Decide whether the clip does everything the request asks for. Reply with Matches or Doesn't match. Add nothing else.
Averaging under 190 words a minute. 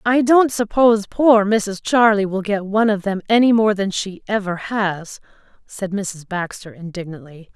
Matches